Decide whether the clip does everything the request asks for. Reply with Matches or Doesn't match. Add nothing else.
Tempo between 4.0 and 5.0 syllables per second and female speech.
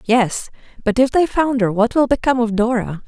Doesn't match